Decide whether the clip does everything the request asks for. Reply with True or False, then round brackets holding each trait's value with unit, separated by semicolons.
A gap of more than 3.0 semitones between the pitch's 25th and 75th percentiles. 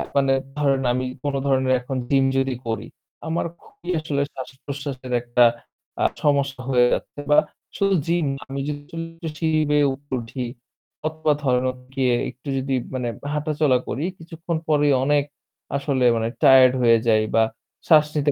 False (2.5 semitones)